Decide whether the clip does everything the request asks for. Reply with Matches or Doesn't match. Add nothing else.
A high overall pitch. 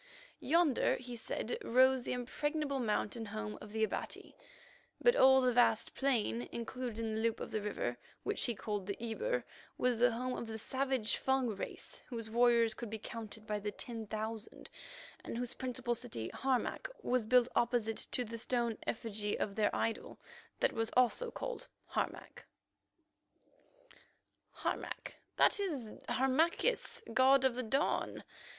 Matches